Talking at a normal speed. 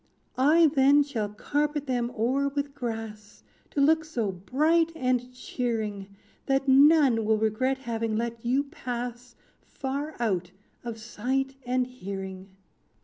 No: slow, 130 wpm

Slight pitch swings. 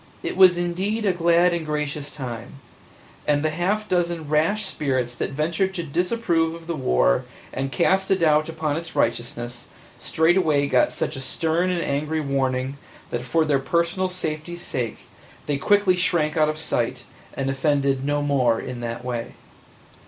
No: average, 4.3 semitones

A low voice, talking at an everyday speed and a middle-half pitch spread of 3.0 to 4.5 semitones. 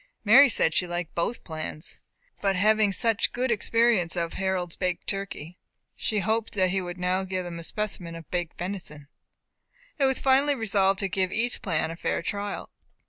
No: high, 190 Hz; average, 180 wpm; average, 3.7 semitones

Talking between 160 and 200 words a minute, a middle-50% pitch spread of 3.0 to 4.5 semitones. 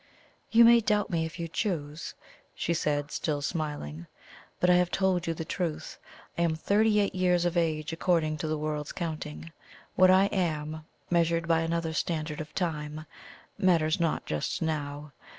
No: average, 170 wpm; narrow, 2.6 semitones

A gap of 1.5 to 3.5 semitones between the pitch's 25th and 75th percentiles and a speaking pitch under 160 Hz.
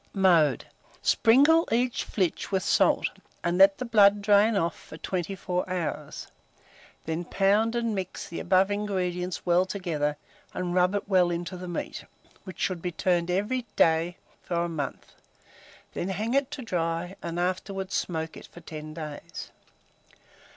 No: average, 3.0 semitones; medium, 185 Hz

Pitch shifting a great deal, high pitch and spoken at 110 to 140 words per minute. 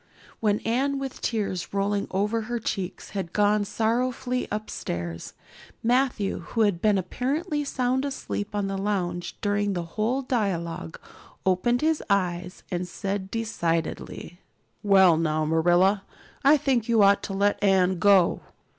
No: average, 4.2 semitones; high, 205 Hz; slow, 135 wpm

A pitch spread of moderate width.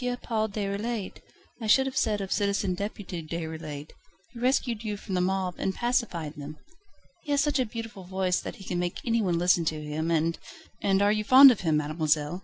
Yes: average, 4.8 semitones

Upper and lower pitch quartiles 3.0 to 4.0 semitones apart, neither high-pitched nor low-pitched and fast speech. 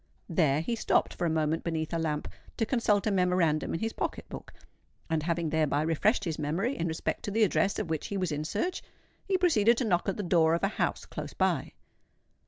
No: average, 4.6 semitones; medium, 170 Hz; fast, 220 wpm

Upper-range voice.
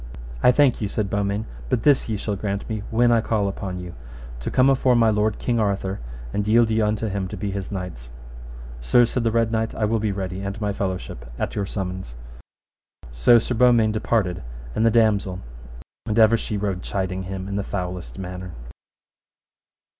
No: low, 105 Hz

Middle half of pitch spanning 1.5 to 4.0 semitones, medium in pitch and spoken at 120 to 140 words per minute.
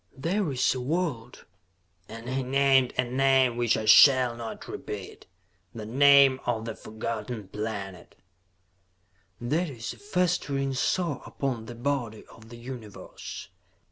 No: average, 3.4 semitones; low, 125 Hz; slow, 135 wpm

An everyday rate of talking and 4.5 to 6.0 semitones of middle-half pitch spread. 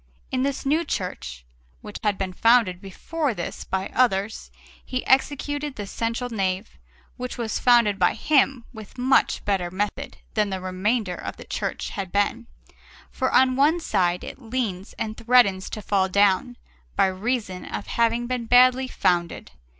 Yes: average, 160 wpm; average, 5.0 semitones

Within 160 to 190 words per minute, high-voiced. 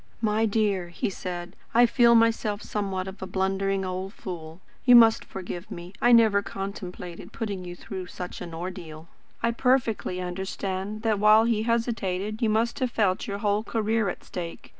Yes: average, 170 wpm; high, 200 Hz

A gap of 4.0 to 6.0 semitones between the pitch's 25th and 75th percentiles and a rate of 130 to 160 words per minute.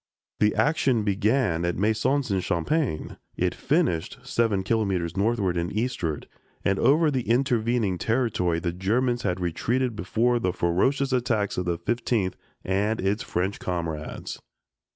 Yes: average, 5.3 semitones; slow, 135 wpm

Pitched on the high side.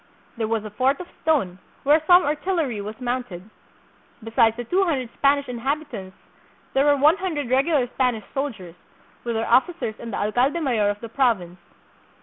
Yes: very high, 250 Hz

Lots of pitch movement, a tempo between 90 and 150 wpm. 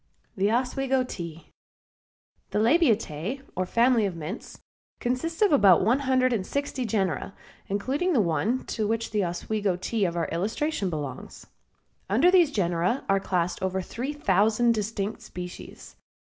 Yes: wide, 5.7 semitones; average, 145 wpm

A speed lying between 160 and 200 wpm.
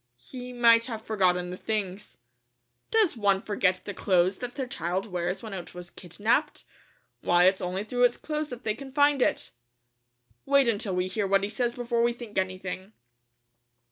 Yes: average, 175 wpm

